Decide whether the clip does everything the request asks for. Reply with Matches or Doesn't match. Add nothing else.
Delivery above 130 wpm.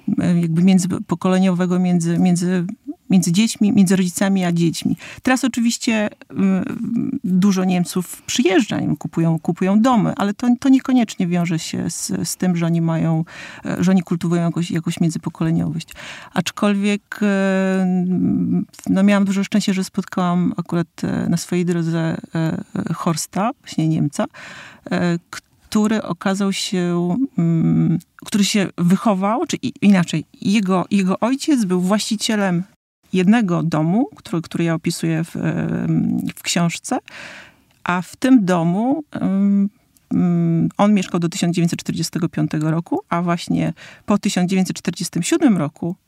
Doesn't match